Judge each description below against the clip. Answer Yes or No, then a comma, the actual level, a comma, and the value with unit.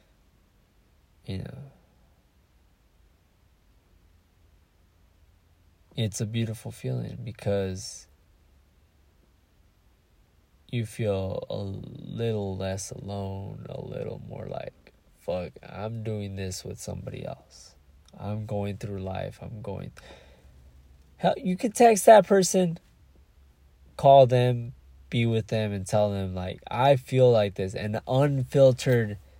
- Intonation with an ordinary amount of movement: No, wide, 6.1 semitones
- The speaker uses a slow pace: Yes, slow, 105 wpm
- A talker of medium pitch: No, very low, 95 Hz